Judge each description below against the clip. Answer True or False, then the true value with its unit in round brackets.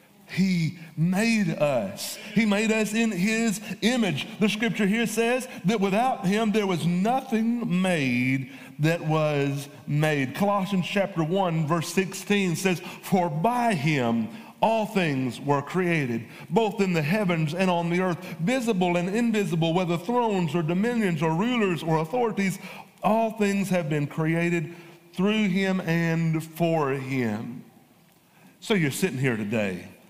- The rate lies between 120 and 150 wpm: True (140 wpm)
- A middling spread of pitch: True (4.4 semitones)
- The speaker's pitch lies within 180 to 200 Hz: True (185 Hz)